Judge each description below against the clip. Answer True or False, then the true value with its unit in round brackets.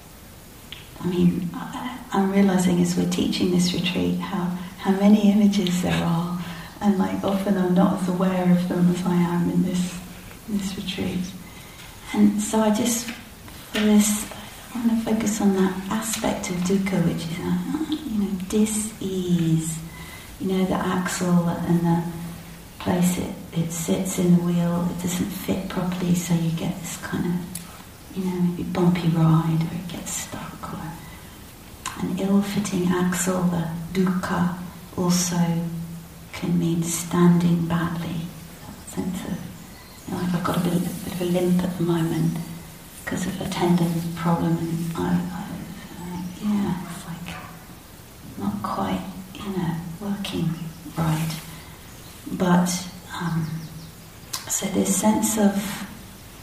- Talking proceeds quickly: False (145 wpm)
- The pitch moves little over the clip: True (2.3 semitones)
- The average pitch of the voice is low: False (180 Hz)